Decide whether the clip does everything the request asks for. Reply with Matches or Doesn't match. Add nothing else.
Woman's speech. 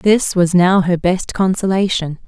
Matches